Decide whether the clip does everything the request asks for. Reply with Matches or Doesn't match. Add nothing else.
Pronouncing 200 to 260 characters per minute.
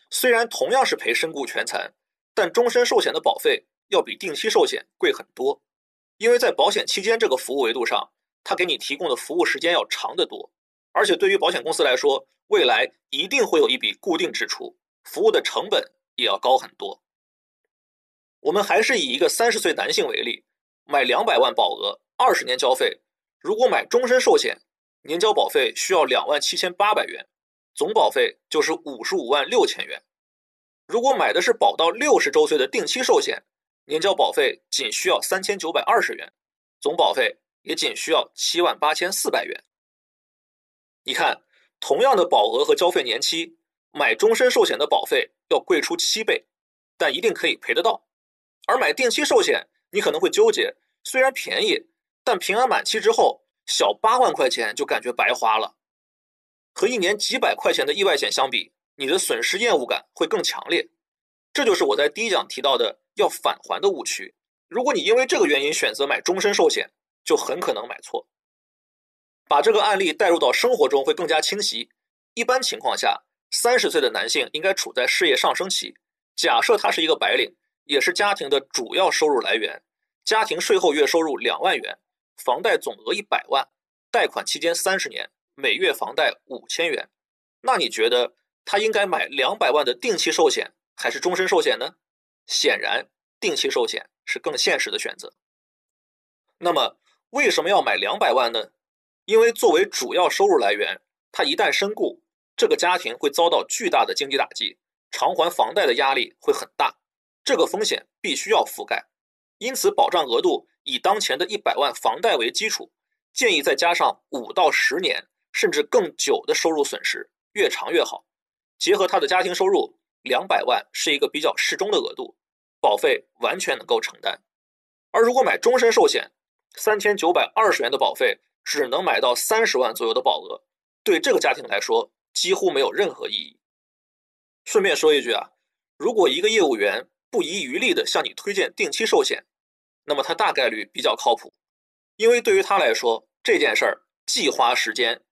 Doesn't match